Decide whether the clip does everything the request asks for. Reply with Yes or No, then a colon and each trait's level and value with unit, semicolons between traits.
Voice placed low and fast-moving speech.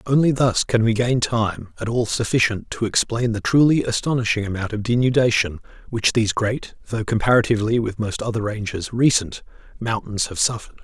No: low, 115 Hz; average, 165 wpm